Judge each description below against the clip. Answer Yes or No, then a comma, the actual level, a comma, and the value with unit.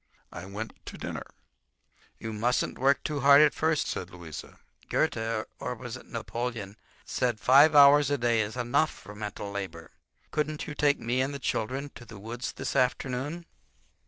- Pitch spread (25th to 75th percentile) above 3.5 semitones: Yes, average, 4.8 semitones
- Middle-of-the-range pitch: No, low, 125 Hz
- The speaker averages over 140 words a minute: Yes, average, 160 wpm